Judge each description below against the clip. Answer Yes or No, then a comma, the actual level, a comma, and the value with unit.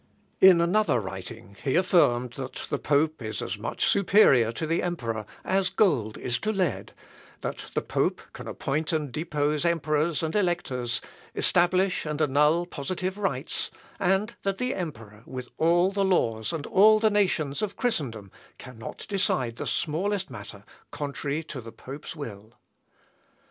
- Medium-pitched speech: Yes, medium, 155 Hz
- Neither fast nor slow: Yes, average, 150 wpm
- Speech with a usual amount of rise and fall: No, wide, 6.9 semitones